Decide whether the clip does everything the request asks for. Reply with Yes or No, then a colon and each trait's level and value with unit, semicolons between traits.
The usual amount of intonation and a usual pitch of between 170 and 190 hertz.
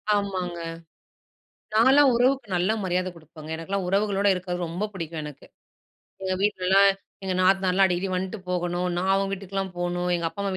No: narrow, 1.9 semitones; medium, 185 Hz